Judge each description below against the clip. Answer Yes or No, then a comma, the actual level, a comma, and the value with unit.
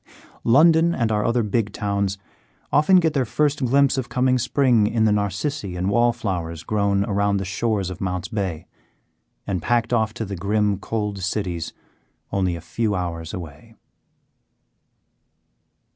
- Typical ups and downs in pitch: Yes, average, 4.1 semitones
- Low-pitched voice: Yes, low, 105 Hz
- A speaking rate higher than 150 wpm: No, average, 145 wpm